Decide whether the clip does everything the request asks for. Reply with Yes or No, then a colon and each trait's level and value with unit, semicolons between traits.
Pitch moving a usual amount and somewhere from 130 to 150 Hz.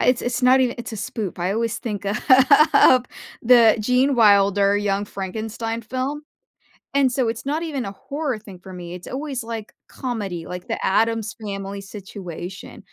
No: average, 4.1 semitones; high, 220 Hz